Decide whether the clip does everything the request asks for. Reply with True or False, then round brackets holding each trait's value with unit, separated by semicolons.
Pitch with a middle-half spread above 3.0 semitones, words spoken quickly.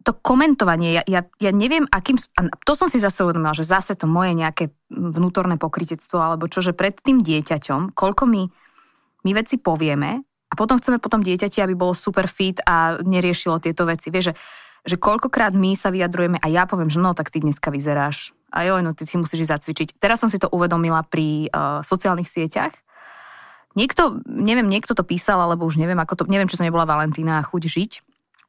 True (3.5 semitones; 200 wpm)